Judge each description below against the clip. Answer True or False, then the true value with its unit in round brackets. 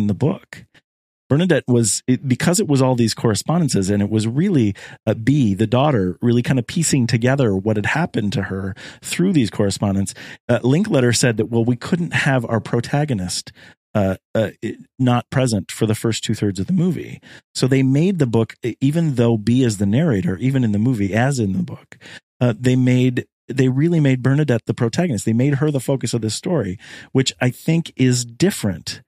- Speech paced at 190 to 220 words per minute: True (200 wpm)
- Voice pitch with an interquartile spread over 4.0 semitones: False (3.7 semitones)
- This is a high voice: False (125 Hz)